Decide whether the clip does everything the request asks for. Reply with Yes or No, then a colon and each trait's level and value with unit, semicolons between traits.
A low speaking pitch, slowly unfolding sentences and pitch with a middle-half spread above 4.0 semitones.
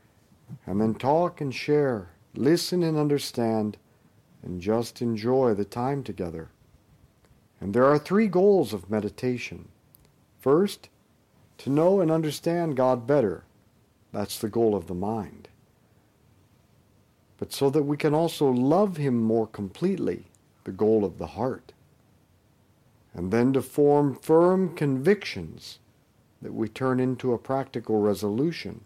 Yes: low, 125 Hz; slow, 130 wpm; wide, 5.5 semitones